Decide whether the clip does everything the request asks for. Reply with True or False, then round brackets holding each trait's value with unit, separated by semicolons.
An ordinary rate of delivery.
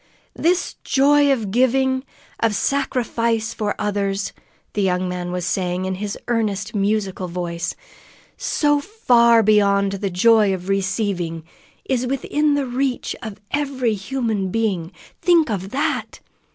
False (130 wpm)